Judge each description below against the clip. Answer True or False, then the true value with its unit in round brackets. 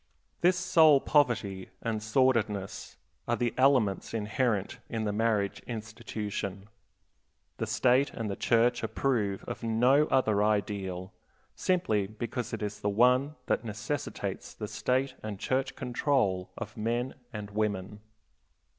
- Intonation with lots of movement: False (3.7 semitones)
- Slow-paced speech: True (130 wpm)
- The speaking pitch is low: True (115 Hz)